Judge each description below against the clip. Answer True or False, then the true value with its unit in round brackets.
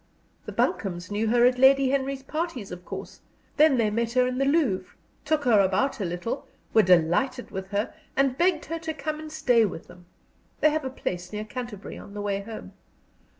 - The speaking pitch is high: True (245 Hz)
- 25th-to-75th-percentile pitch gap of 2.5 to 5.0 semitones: False (5.5 semitones)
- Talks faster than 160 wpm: True (200 wpm)